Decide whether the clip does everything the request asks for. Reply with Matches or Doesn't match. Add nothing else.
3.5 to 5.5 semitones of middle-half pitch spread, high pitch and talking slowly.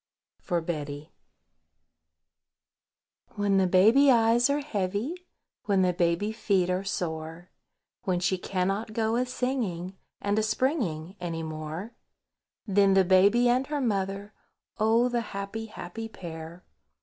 Matches